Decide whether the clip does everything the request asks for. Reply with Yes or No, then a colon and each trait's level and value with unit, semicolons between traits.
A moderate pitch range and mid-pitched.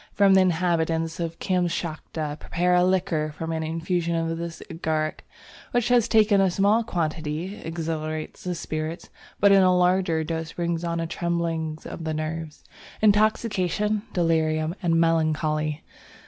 No: narrow, 2.3 semitones; medium, 165 Hz